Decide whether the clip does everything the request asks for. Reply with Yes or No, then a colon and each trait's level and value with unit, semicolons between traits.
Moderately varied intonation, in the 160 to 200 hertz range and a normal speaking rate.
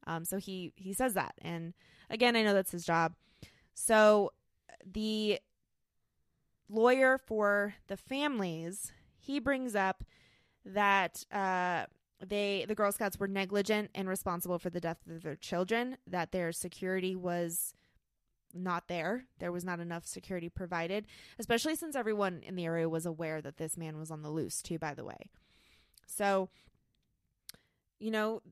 Yes: average, 3.8 semitones; high, 190 Hz; average, 150 wpm